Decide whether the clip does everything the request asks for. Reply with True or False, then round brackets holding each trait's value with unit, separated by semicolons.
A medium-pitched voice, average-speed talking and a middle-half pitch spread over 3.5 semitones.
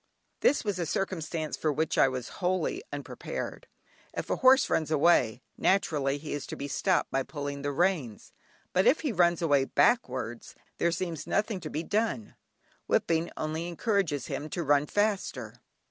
True (160 Hz; 165 wpm; 4.7 semitones)